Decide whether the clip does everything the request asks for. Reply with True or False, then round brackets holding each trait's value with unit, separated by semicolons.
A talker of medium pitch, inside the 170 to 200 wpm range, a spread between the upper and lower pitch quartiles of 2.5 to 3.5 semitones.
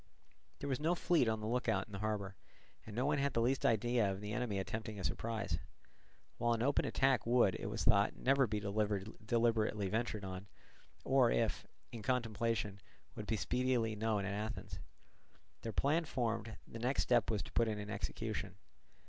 False (110 Hz; 185 wpm; 2.9 semitones)